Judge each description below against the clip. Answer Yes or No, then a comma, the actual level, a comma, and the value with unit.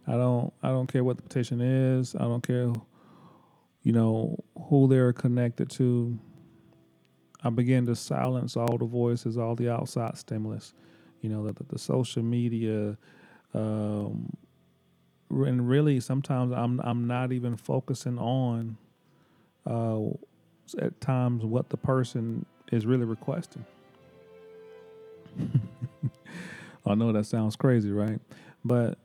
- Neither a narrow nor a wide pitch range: No, narrow, 2.3 semitones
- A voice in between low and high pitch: No, low, 120 Hz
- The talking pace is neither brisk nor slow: No, slow, 130 wpm